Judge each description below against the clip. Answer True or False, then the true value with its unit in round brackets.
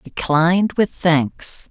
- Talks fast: False (105 wpm)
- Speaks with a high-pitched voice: False (170 Hz)